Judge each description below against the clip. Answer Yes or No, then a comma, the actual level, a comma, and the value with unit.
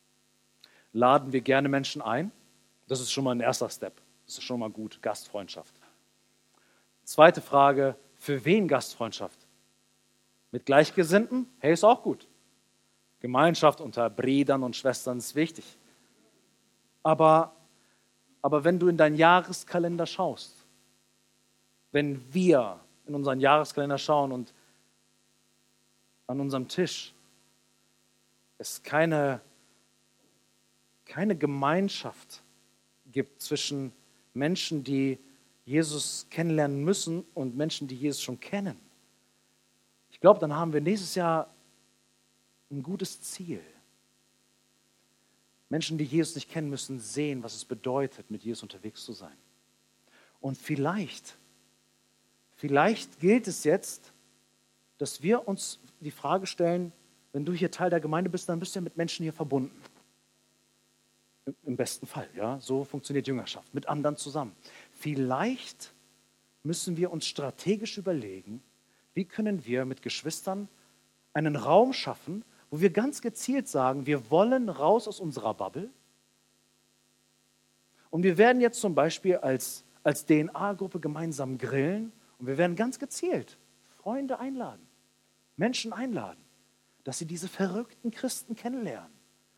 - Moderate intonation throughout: No, wide, 6.2 semitones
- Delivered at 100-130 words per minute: Yes, slow, 125 wpm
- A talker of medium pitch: Yes, medium, 145 Hz